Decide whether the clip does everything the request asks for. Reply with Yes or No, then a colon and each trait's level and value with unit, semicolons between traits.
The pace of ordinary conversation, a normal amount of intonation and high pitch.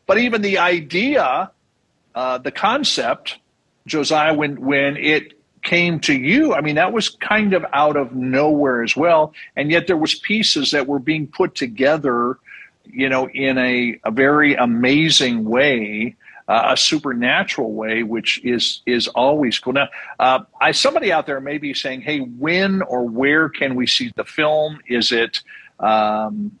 No: average, 165 wpm; average, 4.0 semitones; medium, 140 Hz